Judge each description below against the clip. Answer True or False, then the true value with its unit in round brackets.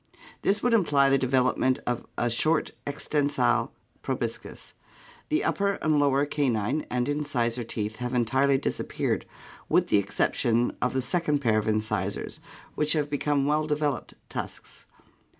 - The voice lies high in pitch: False (140 Hz)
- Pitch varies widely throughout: False (3.6 semitones)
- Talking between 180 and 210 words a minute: False (150 wpm)